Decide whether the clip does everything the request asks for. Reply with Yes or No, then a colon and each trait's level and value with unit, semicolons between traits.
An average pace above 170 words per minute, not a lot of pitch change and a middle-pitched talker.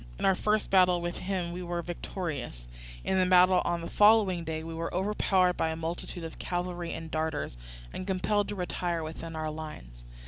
Yes: average, 195 wpm; narrow, 2.3 semitones; medium, 175 Hz